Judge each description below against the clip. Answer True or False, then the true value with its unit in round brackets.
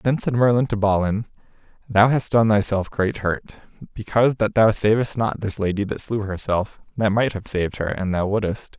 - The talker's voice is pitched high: False (105 Hz)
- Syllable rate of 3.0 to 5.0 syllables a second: False (5.2 syllables/s)